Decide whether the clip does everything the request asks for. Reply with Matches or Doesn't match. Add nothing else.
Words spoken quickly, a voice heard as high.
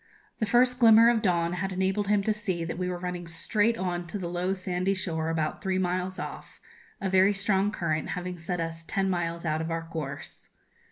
Doesn't match